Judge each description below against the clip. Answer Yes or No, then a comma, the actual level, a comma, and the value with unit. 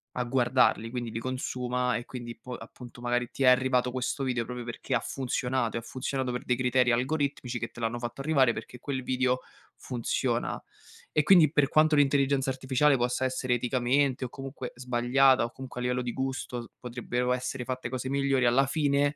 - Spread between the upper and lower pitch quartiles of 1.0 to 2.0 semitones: Yes, narrow, 1.6 semitones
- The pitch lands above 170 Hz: No, low, 125 Hz